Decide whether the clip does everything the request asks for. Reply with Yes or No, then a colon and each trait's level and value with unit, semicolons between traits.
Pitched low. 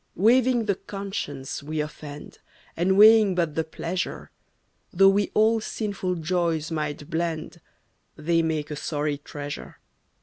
No: medium, 170 Hz